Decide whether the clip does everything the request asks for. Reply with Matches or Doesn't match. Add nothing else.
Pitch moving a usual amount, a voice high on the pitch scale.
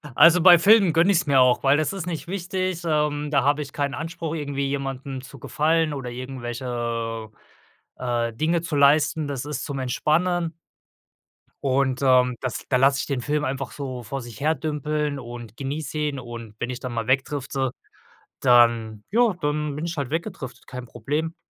Doesn't match